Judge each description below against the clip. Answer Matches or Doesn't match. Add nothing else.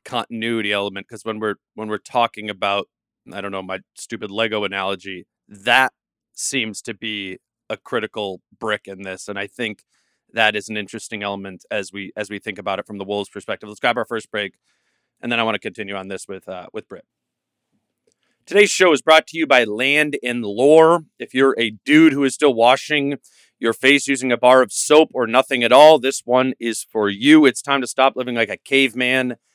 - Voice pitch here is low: Matches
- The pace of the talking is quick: Matches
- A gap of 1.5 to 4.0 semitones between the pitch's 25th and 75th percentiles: Doesn't match